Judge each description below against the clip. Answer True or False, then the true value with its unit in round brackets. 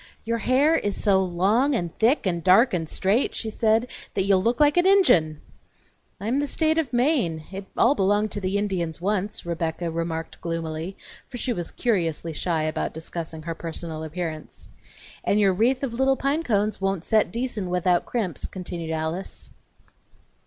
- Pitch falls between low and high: False (195 Hz)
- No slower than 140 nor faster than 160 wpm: False (175 wpm)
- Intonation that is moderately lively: False (5.8 semitones)